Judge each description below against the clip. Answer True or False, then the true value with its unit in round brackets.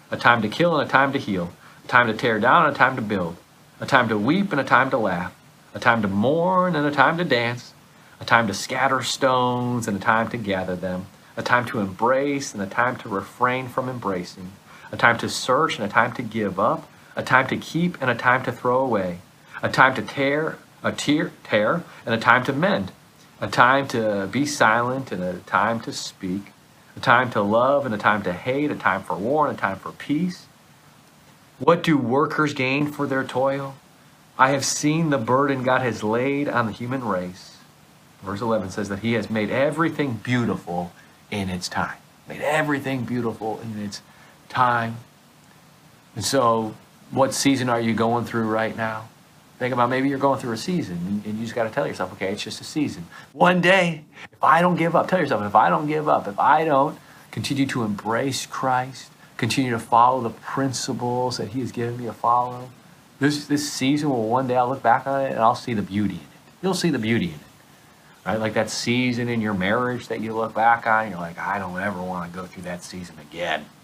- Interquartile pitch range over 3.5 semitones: True (4.0 semitones)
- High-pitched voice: False (120 Hz)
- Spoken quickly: True (215 wpm)